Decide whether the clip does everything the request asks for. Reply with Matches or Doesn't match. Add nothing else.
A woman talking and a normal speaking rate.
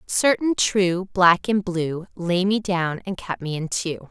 Matches